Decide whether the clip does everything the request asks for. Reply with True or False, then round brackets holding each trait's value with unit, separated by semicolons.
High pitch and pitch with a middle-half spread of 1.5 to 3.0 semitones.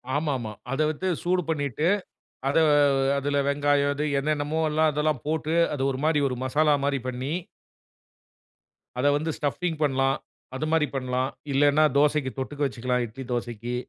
False (145 Hz; 2.7 semitones)